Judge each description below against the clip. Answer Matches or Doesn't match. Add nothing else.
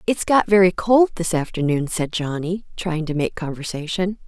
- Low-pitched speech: Doesn't match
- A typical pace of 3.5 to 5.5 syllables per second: Matches